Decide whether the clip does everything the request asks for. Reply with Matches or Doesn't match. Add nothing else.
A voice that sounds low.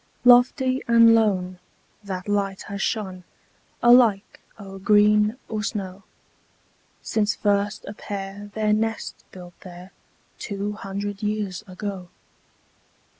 Doesn't match